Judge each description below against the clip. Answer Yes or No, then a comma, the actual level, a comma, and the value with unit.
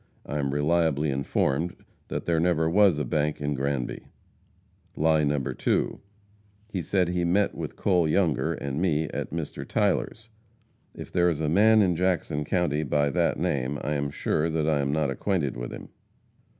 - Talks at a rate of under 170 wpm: No, average, 175 wpm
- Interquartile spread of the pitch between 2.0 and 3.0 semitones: No, average, 3.4 semitones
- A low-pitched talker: Yes, very low, 80 Hz